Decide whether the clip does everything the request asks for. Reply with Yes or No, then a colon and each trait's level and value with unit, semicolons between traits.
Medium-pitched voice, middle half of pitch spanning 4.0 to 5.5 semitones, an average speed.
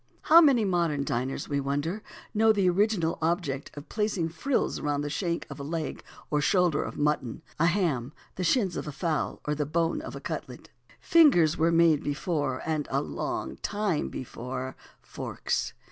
Yes: medium, 165 Hz; average, 4.3 semitones; average, 175 wpm